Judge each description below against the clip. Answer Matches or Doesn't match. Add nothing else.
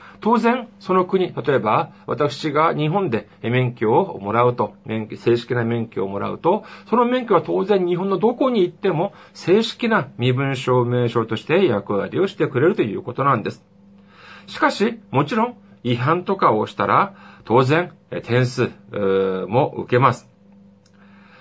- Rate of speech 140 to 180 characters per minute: Doesn't match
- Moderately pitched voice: Doesn't match